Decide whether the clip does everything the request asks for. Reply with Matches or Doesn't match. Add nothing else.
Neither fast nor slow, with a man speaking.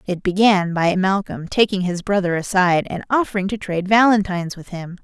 Doesn't match